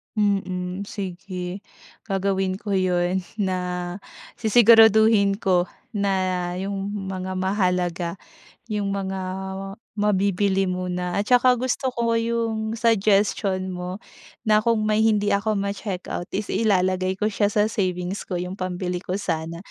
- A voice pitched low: No, high, 195 Hz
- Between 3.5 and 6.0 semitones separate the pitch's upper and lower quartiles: No, narrow, 2.5 semitones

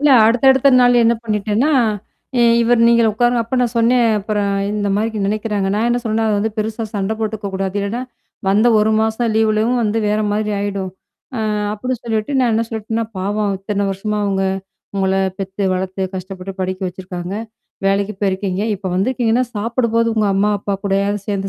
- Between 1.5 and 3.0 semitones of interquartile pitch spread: Yes, average, 2.7 semitones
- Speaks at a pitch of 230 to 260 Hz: No, high, 210 Hz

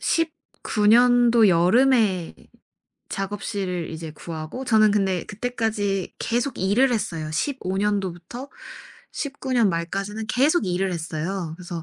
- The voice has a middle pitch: No, high, 205 Hz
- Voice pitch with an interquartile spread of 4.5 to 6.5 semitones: Yes, average, 5.3 semitones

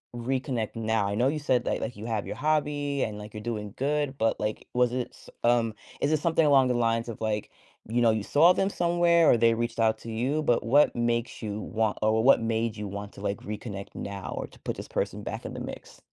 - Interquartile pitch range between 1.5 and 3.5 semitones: No, average, 4.0 semitones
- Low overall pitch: Yes, low, 115 Hz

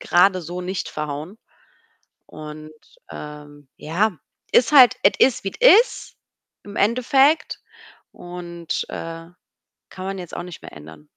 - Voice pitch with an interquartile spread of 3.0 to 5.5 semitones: Yes, average, 5.1 semitones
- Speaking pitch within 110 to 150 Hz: No, medium, 175 Hz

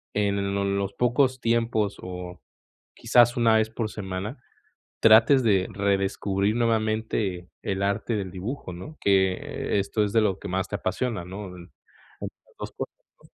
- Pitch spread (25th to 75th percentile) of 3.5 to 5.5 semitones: No, average, 2.8 semitones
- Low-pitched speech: Yes, low, 100 Hz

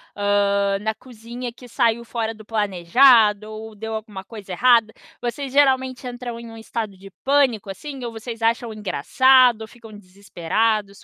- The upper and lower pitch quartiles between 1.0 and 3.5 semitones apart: Yes, average, 2.9 semitones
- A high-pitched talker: Yes, high, 225 Hz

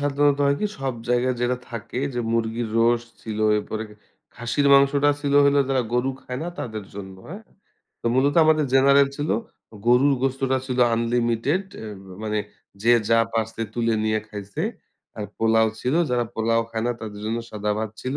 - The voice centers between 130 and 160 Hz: No, low, 120 Hz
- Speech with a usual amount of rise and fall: Yes, average, 3.5 semitones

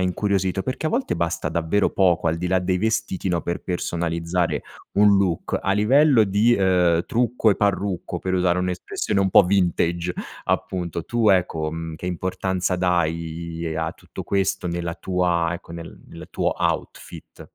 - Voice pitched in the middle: No, very low, 90 Hz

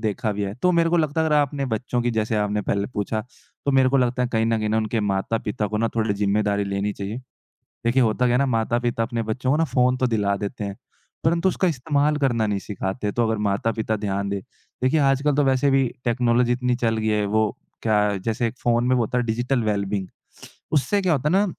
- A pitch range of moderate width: Yes, average, 3.9 semitones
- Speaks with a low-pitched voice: Yes, low, 115 Hz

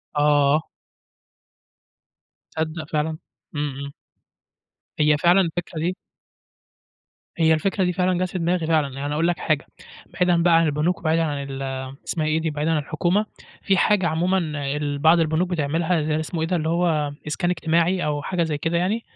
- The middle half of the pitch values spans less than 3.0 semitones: Yes, narrow, 2.6 semitones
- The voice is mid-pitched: Yes, medium, 160 Hz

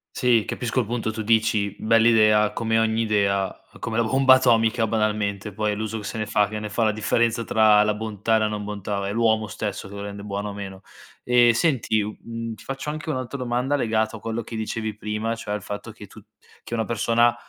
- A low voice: Yes, low, 110 Hz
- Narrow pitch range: Yes, narrow, 1.8 semitones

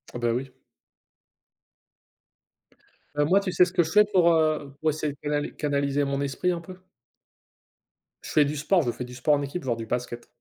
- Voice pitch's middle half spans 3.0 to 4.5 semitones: Yes, average, 3.8 semitones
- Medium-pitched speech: Yes, medium, 145 Hz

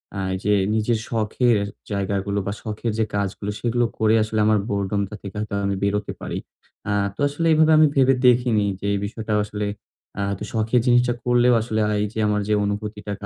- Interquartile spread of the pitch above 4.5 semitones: No, average, 2.9 semitones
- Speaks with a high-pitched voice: No, low, 110 Hz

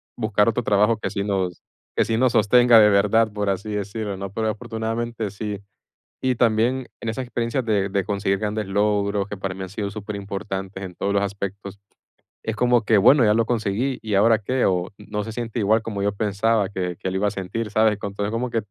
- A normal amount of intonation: No, narrow, 2.3 semitones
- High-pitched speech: No, low, 105 Hz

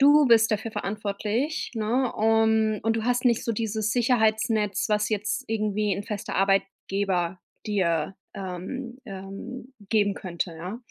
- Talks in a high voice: Yes, high, 215 Hz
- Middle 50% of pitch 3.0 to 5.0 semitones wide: No, narrow, 2.5 semitones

